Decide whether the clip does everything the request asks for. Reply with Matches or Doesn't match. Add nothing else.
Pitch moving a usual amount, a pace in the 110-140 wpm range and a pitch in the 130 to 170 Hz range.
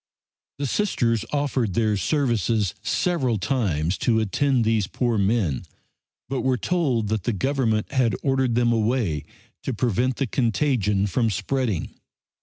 Doesn't match